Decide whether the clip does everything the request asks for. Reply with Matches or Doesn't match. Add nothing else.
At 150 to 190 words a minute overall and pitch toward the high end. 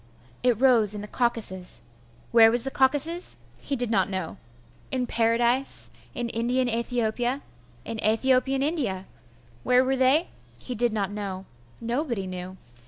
Doesn't match